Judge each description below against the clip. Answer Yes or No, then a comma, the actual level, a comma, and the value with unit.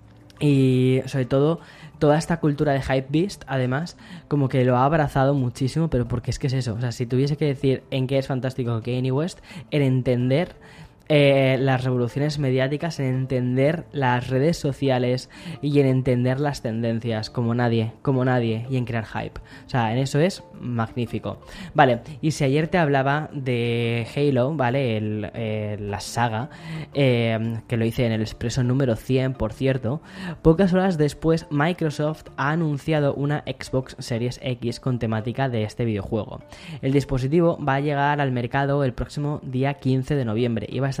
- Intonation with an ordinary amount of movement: Yes, average, 3.2 semitones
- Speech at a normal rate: Yes, average, 180 wpm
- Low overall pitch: Yes, low, 130 Hz